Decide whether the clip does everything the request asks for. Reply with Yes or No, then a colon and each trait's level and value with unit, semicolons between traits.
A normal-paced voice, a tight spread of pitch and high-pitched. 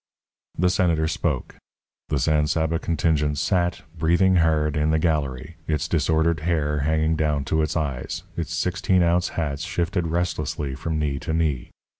No: average, 155 wpm; narrow, 2.1 semitones; very low, 80 Hz